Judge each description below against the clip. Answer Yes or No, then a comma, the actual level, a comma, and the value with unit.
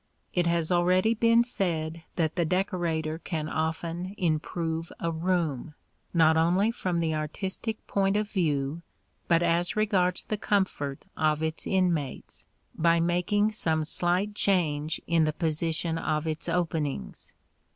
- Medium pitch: Yes, medium, 170 Hz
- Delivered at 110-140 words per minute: Yes, slow, 135 wpm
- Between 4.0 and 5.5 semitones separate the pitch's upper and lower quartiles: No, average, 2.7 semitones